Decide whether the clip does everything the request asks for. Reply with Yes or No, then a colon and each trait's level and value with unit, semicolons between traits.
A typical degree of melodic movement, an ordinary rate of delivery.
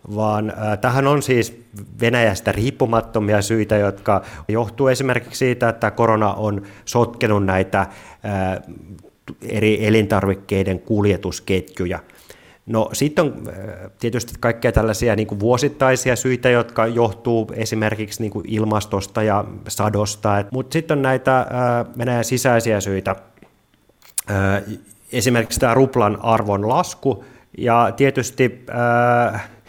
Yes: average, 3.0 semitones; average, 115 wpm